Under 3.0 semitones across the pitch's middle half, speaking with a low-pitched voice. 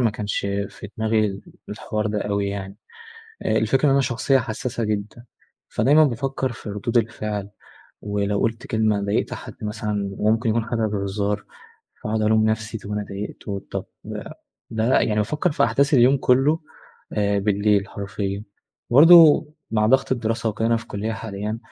Yes: narrow, 2.5 semitones; low, 110 Hz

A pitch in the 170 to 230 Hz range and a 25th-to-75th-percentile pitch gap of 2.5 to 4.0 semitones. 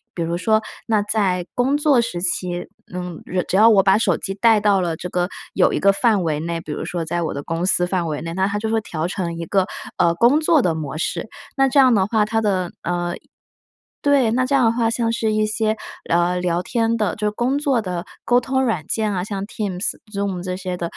No: high, 200 Hz; average, 4.4 semitones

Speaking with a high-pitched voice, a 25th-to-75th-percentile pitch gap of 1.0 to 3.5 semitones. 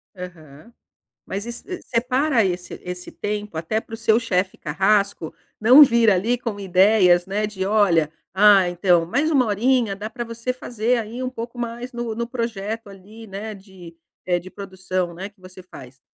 No: high, 210 Hz; average, 4.0 semitones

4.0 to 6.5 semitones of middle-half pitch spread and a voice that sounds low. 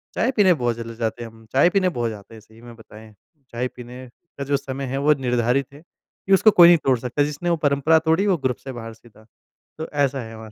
Yes: average, 4.6 semitones; low, 130 Hz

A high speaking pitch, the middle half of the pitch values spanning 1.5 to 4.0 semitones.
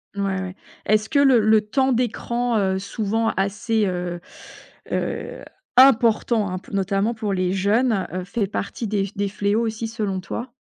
Yes: high, 210 Hz; average, 2.9 semitones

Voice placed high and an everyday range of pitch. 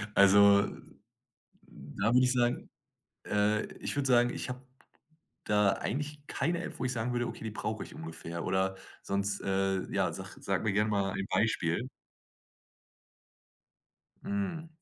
No: low, 105 Hz; average, 4.4 semitones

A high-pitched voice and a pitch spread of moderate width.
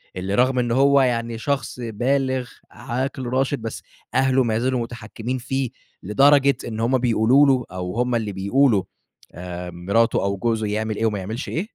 No: low, 120 Hz; average, 3.3 semitones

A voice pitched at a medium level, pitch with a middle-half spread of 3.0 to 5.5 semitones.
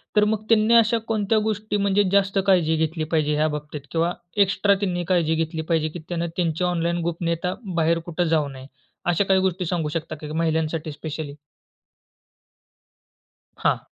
Yes: medium, 170 Hz; average, 3.4 semitones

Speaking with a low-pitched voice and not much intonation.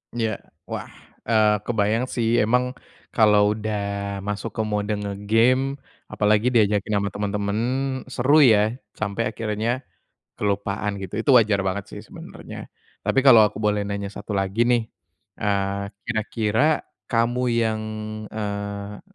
Yes: low, 105 Hz; narrow, 2.0 semitones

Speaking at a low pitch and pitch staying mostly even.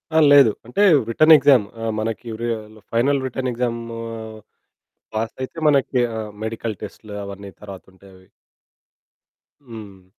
No: low, 115 Hz; average, 3.6 semitones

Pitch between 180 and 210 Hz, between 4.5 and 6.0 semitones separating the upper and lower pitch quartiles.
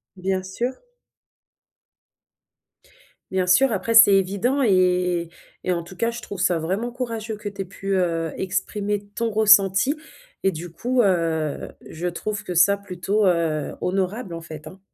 No: high, 190 Hz; average, 3.2 semitones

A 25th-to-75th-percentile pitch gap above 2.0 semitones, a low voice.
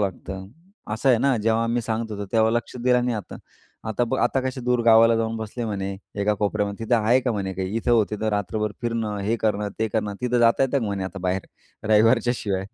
Yes: narrow, 2.5 semitones; low, 110 Hz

